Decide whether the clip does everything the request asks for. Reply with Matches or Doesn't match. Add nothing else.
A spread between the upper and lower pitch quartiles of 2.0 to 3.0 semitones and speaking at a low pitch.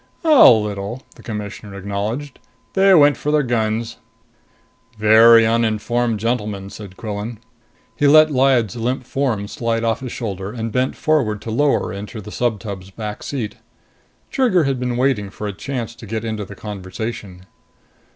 Doesn't match